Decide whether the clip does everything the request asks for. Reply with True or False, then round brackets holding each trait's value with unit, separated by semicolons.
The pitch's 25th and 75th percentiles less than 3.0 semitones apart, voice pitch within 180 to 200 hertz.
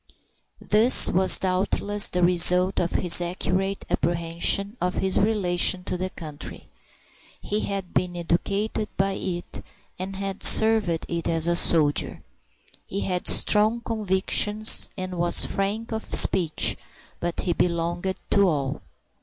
True (2.5 semitones; 185 Hz)